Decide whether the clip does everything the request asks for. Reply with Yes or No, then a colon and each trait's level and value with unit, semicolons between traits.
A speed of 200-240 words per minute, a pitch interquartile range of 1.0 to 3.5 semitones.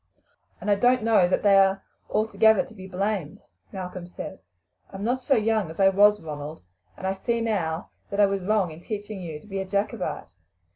Yes: fast, 205 wpm; average, 2.8 semitones